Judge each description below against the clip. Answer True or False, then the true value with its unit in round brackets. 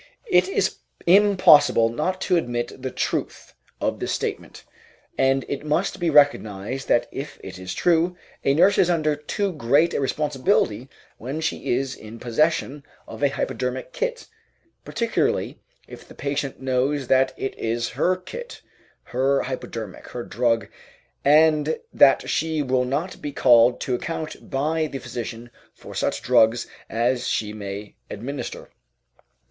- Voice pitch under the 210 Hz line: True (135 Hz)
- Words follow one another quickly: False (145 wpm)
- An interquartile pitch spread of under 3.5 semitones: False (4.7 semitones)